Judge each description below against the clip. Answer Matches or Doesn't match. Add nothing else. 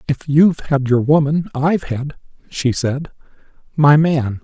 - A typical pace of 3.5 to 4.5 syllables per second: Matches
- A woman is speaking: Doesn't match